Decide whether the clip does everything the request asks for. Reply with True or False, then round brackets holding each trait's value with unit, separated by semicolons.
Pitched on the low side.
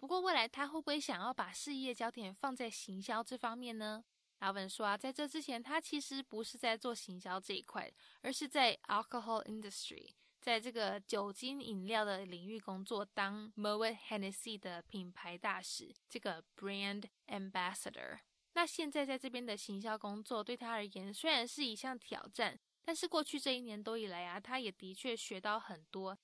False (225 Hz)